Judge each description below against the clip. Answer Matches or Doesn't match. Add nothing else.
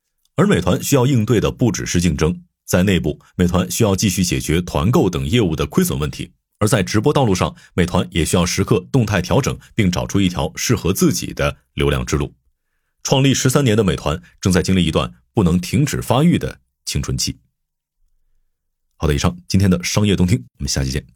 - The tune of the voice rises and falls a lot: Matches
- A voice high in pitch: Doesn't match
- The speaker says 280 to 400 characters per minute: Matches